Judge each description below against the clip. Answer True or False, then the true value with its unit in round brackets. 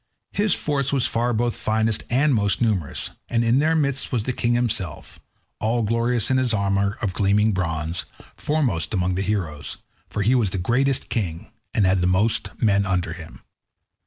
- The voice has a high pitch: False (110 Hz)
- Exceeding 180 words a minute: False (170 wpm)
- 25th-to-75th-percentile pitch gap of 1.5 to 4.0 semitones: False (4.5 semitones)